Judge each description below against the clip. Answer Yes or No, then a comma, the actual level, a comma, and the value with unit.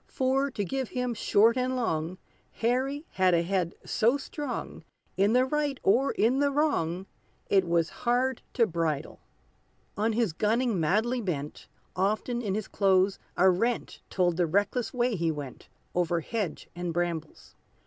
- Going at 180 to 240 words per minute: No, average, 155 wpm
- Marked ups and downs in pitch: Yes, wide, 6.2 semitones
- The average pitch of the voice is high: Yes, high, 210 Hz